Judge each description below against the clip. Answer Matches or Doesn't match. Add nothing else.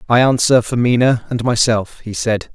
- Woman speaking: Doesn't match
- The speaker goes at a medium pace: Matches